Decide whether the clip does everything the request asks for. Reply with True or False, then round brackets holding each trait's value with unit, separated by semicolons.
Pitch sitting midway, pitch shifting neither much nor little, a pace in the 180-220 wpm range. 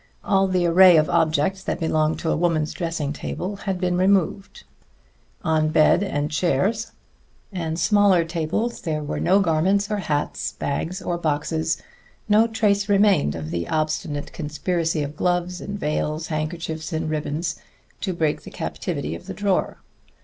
False (165 Hz; 3.7 semitones; 155 wpm)